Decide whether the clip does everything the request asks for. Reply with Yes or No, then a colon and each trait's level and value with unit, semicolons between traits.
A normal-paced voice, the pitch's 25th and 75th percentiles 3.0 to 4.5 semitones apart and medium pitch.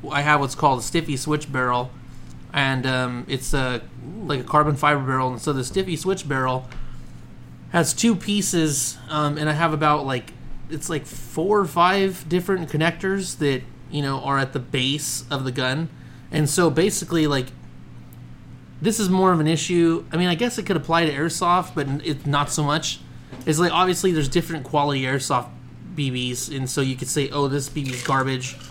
Yes: average, 190 wpm; average, 4.2 semitones; medium, 145 Hz